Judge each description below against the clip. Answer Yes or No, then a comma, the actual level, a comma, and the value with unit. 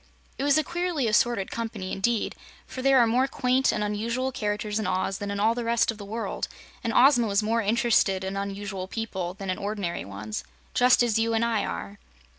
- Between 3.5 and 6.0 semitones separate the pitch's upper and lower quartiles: No, average, 3.1 semitones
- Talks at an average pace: No, fast, 210 wpm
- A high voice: Yes, high, 220 Hz